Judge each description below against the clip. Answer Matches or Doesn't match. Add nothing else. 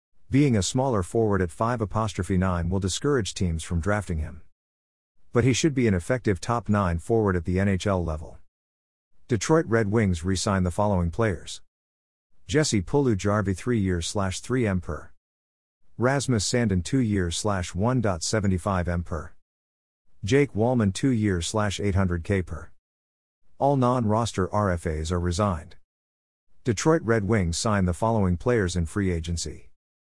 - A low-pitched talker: Matches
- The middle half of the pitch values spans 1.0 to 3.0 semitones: Doesn't match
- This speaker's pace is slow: Doesn't match